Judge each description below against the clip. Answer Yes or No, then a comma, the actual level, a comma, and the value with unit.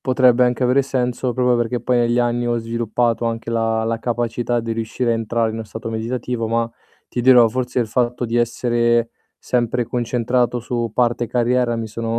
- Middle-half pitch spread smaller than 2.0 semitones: Yes, narrow, 1.3 semitones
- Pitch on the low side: Yes, low, 120 Hz